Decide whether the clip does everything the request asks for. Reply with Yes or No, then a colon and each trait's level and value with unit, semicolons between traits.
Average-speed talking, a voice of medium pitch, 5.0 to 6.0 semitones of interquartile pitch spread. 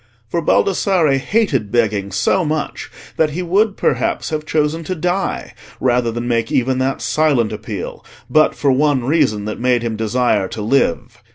No: average, 165 wpm; low, 130 Hz; wide, 5.4 semitones